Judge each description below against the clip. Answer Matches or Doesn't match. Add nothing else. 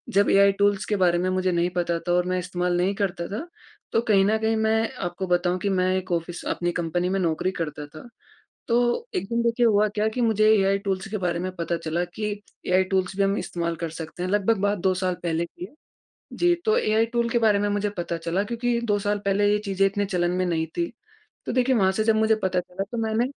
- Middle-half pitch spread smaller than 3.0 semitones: Doesn't match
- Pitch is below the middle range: Doesn't match